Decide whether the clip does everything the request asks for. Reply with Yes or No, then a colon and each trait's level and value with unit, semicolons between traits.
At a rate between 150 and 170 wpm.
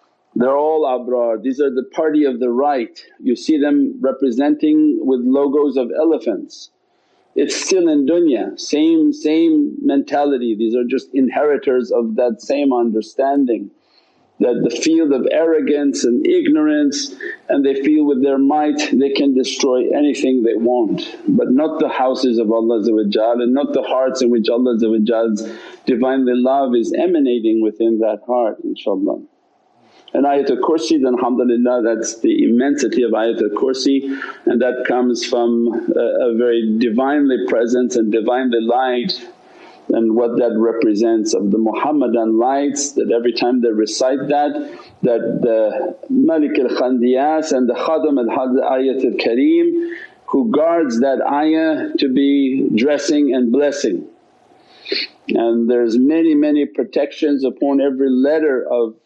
No: average, 140 wpm